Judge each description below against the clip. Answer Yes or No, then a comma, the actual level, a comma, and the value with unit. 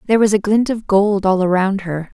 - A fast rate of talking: Yes, fast, 245 wpm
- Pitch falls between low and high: No, high, 200 Hz